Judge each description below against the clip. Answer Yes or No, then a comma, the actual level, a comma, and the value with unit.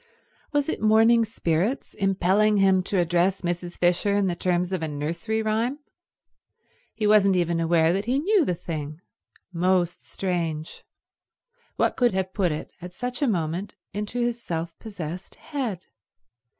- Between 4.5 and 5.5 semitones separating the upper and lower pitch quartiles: No, average, 4.1 semitones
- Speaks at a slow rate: No, average, 150 wpm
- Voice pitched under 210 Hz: Yes, high, 190 Hz